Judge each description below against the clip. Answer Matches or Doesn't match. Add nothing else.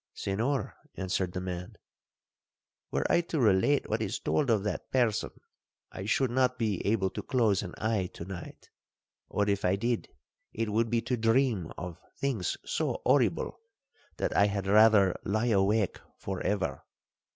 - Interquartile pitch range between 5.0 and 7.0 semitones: Doesn't match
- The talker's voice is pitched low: Matches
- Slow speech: Doesn't match